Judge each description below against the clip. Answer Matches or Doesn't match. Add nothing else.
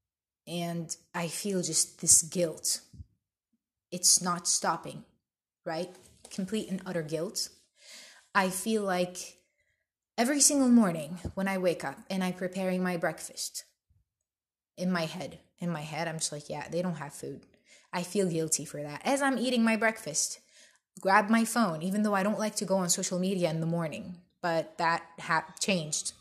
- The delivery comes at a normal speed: Matches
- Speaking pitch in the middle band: Matches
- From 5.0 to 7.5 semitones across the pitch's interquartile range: Doesn't match